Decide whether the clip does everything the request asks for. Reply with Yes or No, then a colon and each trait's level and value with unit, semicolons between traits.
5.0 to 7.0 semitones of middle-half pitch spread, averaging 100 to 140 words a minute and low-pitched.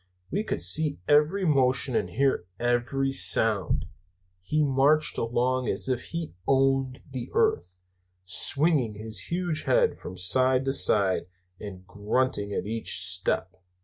Yes: average, 5.3 semitones; slow, 135 wpm; low, 130 Hz